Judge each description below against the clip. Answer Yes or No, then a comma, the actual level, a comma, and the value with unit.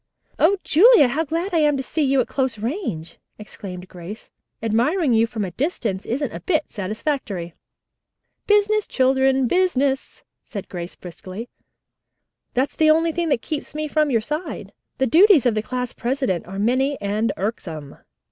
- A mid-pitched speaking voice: No, very high, 260 Hz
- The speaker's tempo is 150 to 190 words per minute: Yes, average, 160 wpm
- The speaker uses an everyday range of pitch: No, wide, 6.4 semitones